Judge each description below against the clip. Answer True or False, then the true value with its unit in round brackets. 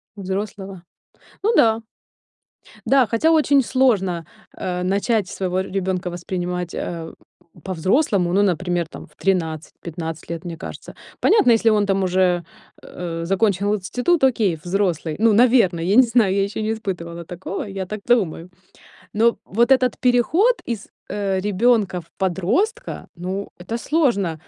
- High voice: True (195 Hz)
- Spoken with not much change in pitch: False (4.4 semitones)